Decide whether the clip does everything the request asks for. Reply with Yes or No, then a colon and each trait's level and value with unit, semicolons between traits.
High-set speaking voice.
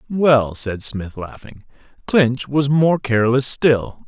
No: low, 125 Hz